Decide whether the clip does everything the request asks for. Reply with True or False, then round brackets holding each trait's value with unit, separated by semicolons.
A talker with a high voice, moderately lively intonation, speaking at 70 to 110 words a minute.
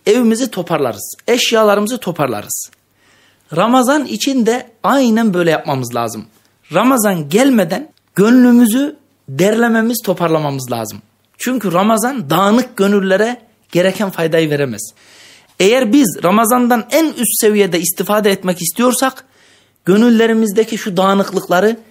False (205 Hz; 5.9 semitones; 100 wpm)